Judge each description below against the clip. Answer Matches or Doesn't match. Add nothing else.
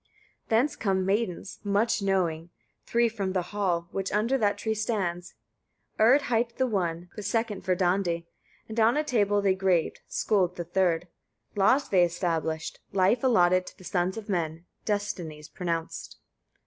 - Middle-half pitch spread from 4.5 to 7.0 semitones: Doesn't match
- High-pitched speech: Matches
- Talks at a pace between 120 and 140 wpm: Doesn't match